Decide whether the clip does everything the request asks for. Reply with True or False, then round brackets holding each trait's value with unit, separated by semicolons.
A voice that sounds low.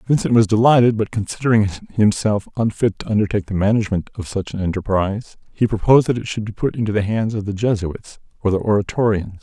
True (105 Hz)